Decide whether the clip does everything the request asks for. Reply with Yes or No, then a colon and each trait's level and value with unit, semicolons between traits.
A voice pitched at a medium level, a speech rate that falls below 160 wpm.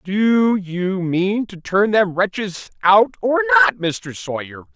No: high, 195 Hz; average, 150 wpm